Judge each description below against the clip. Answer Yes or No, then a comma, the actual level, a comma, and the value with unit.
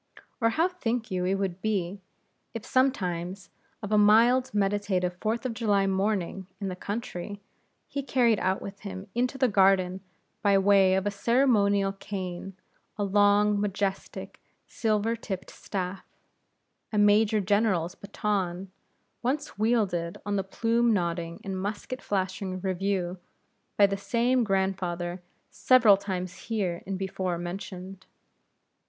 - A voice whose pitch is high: Yes, high, 200 Hz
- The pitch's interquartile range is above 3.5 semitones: No, narrow, 2.6 semitones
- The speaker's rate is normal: No, slow, 130 wpm